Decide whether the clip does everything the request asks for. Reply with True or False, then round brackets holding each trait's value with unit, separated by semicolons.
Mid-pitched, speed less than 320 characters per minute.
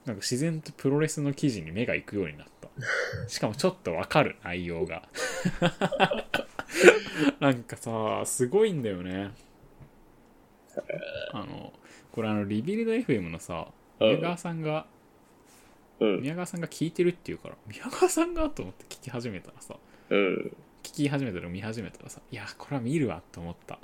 True (145 Hz; 310 characters per minute)